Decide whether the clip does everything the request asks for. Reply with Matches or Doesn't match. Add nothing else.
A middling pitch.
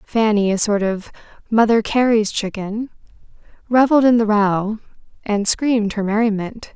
Doesn't match